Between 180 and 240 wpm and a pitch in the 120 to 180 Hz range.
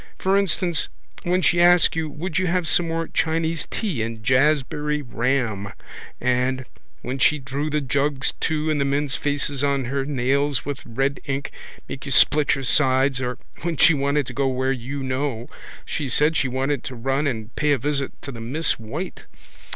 Yes: average, 185 wpm; medium, 140 Hz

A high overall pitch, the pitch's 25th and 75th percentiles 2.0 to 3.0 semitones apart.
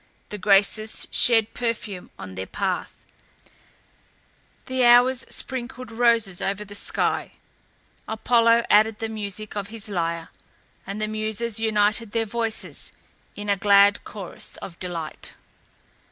Yes: high, 215 Hz; narrow, 2.5 semitones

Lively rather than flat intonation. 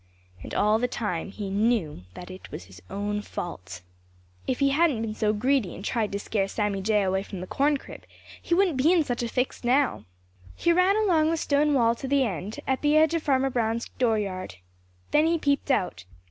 Yes: wide, 6.1 semitones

